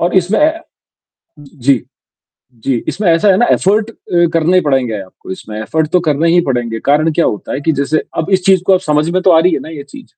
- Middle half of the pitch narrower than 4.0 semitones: No, average, 4.8 semitones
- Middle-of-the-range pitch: Yes, medium, 160 Hz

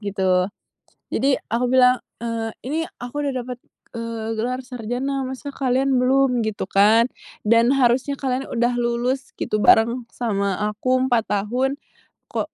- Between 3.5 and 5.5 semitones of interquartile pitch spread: No, narrow, 2.5 semitones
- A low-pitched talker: No, high, 245 Hz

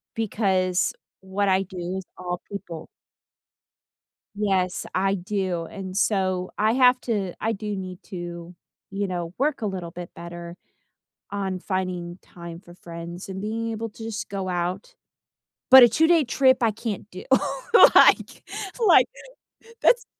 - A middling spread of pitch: Yes, average, 3.2 semitones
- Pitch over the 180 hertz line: Yes, high, 190 Hz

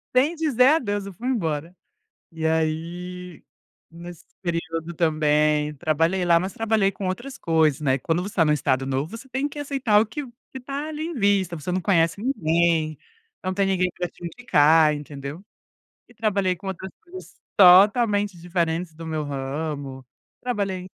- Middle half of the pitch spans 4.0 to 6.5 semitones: Yes, average, 4.7 semitones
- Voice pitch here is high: No, medium, 175 Hz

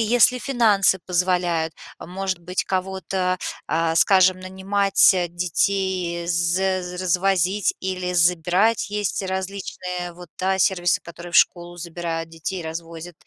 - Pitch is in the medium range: Yes, medium, 180 Hz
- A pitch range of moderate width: No, narrow, 1.7 semitones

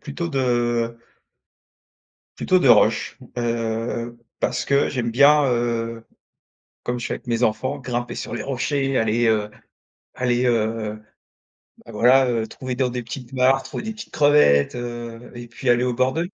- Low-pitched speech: Yes, low, 120 Hz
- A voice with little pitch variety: Yes, narrow, 2.2 semitones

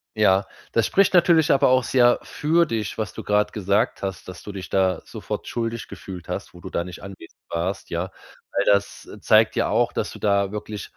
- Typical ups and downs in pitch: Yes, average, 3.7 semitones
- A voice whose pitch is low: Yes, low, 100 Hz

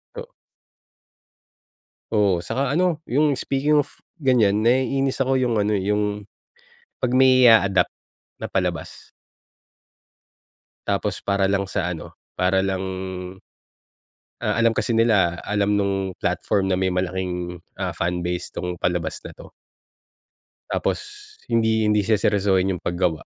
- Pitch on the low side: Yes, low, 105 Hz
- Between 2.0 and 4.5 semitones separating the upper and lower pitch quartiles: No, average, 4.9 semitones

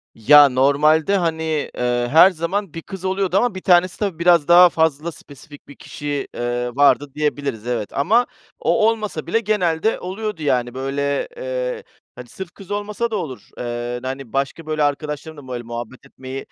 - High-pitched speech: No, medium, 155 Hz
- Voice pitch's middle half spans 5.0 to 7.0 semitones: Yes, wide, 5.6 semitones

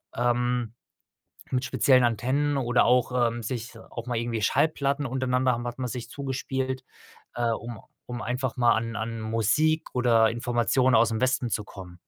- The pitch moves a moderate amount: No, narrow, 2.1 semitones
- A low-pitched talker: Yes, low, 120 Hz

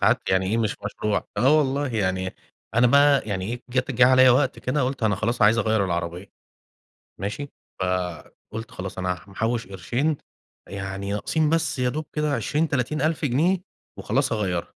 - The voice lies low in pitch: Yes, low, 115 Hz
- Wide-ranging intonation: Yes, wide, 6.0 semitones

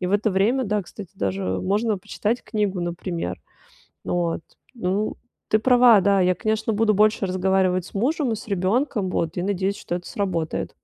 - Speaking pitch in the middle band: No, high, 195 Hz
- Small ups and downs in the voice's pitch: No, average, 3.2 semitones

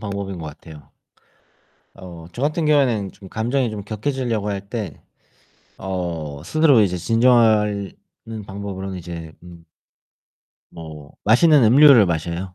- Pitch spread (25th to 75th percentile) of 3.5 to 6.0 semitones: Yes, average, 5.3 semitones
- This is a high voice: No, low, 100 Hz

